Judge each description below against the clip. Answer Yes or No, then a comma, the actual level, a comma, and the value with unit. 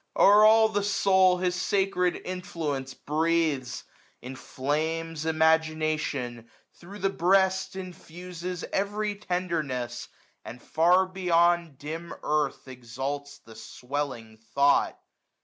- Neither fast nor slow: No, slow, 100 wpm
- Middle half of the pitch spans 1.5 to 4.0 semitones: No, average, 4.5 semitones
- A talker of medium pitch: Yes, medium, 165 Hz